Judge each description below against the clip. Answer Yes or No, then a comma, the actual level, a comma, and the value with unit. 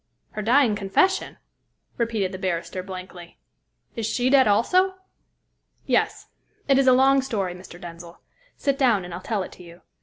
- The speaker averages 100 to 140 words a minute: No, average, 160 wpm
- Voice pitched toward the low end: No, high, 210 Hz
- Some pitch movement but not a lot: No, wide, 6.2 semitones